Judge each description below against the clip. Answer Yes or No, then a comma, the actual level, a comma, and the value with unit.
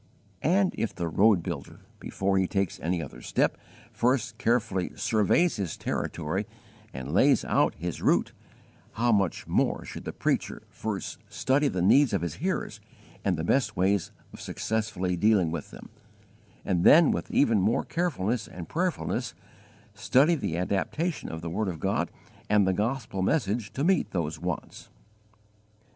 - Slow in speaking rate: No, average, 155 wpm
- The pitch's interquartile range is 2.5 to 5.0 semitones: No, wide, 5.6 semitones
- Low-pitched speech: Yes, low, 100 Hz